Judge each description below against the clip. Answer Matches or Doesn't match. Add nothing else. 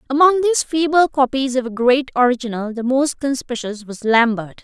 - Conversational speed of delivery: Matches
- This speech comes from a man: Doesn't match